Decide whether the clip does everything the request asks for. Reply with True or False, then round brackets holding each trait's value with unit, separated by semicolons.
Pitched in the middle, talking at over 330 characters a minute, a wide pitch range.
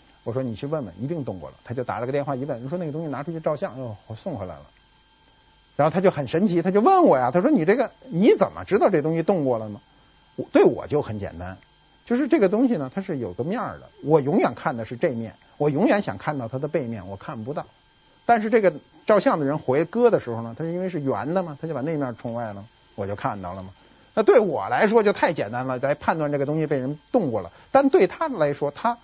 True (145 Hz; 355 characters per minute; 7.8 semitones)